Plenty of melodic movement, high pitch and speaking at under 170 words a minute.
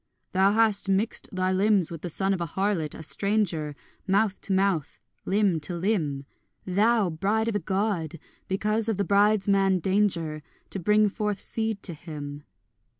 No: average, 3.5 semitones; high, 195 Hz; average, 160 wpm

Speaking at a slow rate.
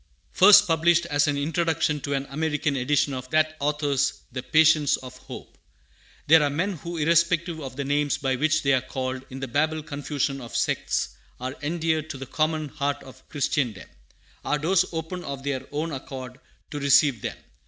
No: average, 180 wpm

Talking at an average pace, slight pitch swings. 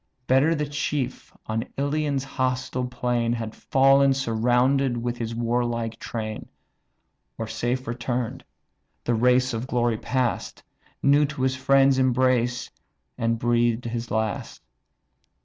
No: slow, 120 wpm; narrow, 2.2 semitones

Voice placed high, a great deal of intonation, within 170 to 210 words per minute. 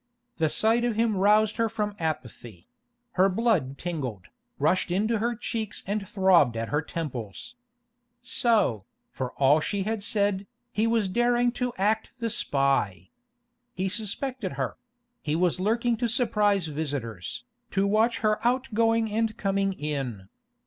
No: high, 200 Hz; wide, 6.8 semitones; average, 140 wpm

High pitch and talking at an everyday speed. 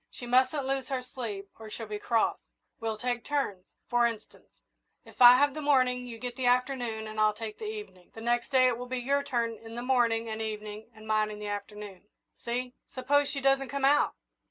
No: high, 240 Hz; fast, 215 wpm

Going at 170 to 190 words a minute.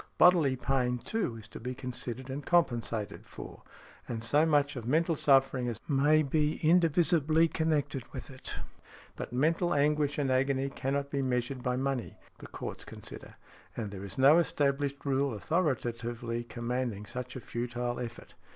No: average, 150 wpm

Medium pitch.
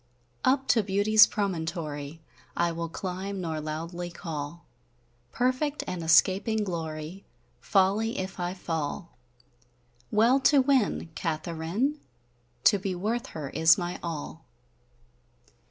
Yes: medium, 180 Hz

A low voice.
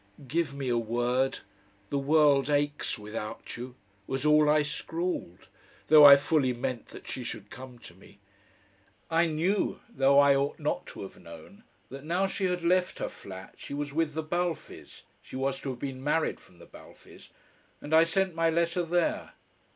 No: medium, 145 Hz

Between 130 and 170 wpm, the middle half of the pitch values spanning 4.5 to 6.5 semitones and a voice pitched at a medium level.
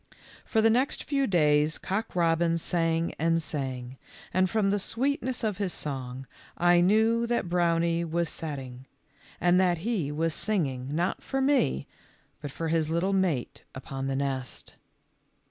Yes: average, 160 wpm; average, 5.0 semitones; medium, 170 Hz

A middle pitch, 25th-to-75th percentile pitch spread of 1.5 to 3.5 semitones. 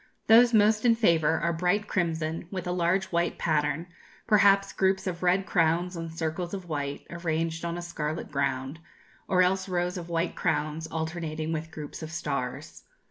Yes: medium, 170 Hz; narrow, 2.5 semitones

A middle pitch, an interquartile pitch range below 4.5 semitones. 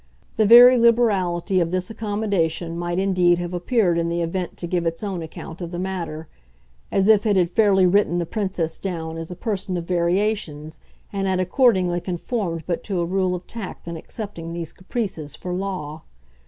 Yes: medium, 180 Hz; average, 2.8 semitones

